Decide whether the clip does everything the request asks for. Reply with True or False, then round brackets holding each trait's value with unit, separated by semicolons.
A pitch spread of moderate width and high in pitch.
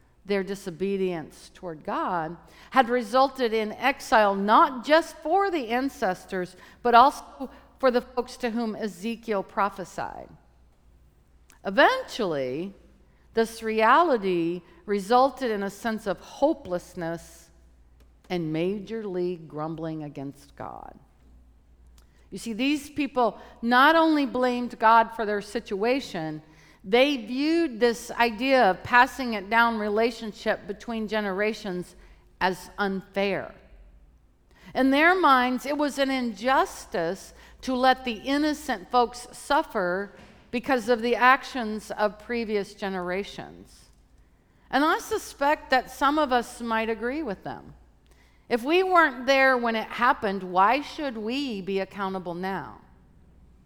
False (5.9 semitones; 225 Hz)